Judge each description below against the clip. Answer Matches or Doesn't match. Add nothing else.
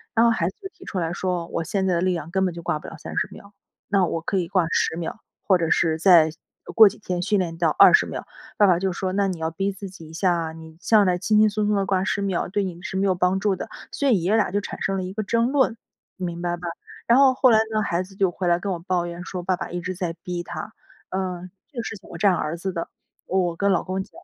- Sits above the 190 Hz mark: Doesn't match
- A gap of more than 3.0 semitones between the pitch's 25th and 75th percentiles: Doesn't match